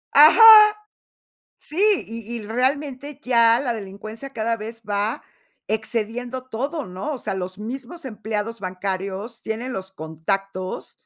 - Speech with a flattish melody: No, average, 4.4 semitones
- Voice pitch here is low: No, high, 225 Hz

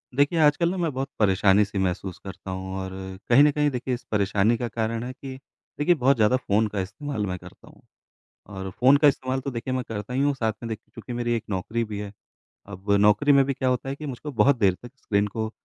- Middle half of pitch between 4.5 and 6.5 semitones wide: Yes, average, 5.0 semitones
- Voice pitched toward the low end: Yes, low, 115 Hz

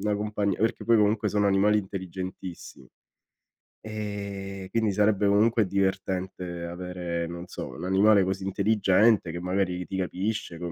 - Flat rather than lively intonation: Yes, narrow, 2.3 semitones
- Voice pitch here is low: Yes, very low, 95 Hz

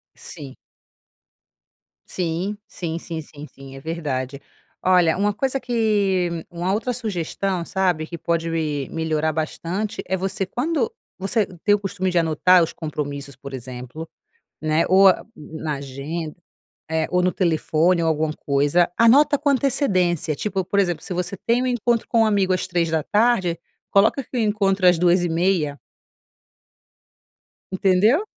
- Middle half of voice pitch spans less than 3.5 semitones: No, average, 4.1 semitones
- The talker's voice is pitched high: No, medium, 175 Hz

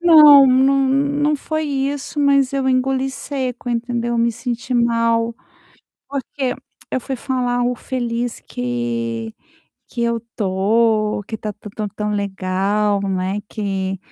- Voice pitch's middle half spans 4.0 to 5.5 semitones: Yes, average, 4.3 semitones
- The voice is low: No, high, 235 Hz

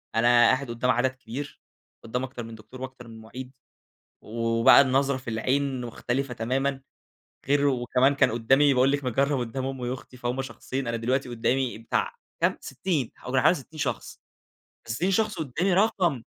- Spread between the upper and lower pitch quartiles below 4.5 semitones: Yes, narrow, 2.5 semitones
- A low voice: Yes, low, 130 Hz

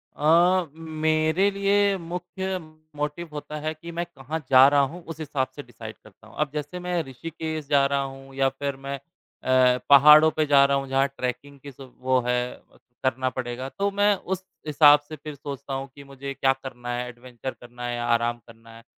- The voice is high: No, medium, 140 Hz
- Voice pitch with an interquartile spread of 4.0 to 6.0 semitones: No, average, 3.4 semitones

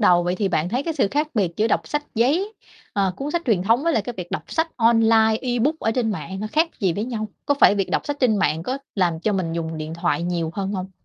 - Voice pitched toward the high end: Yes, high, 215 Hz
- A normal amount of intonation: No, wide, 6.0 semitones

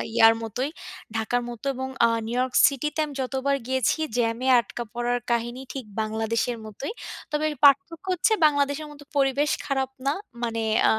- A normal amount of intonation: Yes, average, 3.1 semitones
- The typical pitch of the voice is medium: No, very high, 260 Hz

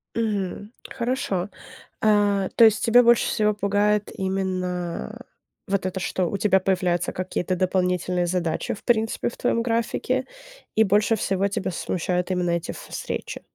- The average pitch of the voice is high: Yes, high, 195 Hz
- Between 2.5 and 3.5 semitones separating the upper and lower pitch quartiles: Yes, average, 2.8 semitones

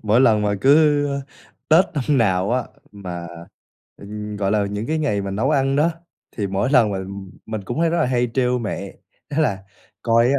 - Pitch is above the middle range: No, low, 115 Hz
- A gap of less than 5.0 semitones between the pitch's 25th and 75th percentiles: No, wide, 5.6 semitones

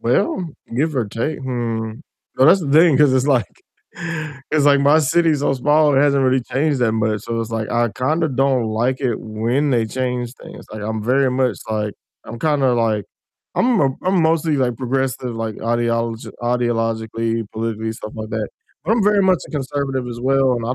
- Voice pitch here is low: Yes, low, 130 Hz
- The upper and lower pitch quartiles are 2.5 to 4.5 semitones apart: Yes, average, 4.1 semitones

